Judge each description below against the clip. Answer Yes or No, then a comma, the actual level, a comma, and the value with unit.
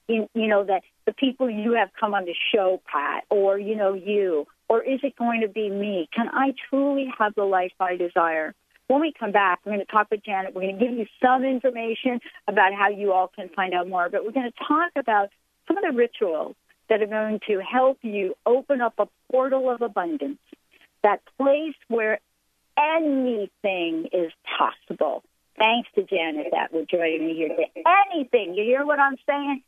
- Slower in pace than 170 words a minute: No, average, 200 wpm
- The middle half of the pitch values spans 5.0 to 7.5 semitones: Yes, wide, 5.4 semitones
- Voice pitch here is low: No, high, 220 Hz